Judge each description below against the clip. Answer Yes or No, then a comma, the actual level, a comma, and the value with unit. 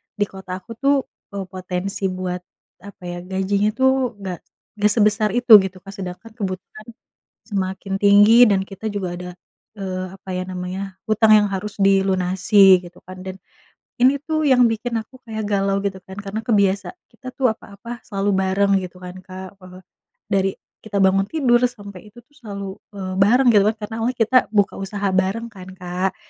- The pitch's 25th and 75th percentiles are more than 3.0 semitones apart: No, average, 2.7 semitones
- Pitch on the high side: Yes, high, 200 Hz